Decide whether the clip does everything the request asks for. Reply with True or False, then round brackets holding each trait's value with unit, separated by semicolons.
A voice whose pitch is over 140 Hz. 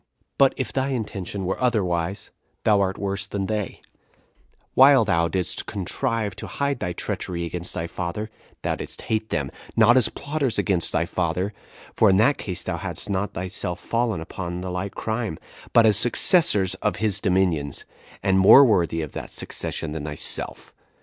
False (100 Hz)